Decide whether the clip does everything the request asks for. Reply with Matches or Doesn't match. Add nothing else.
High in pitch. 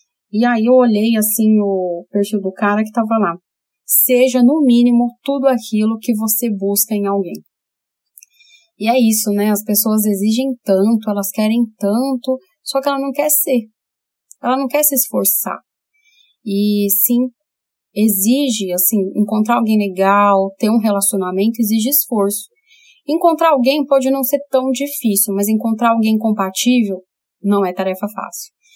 Matches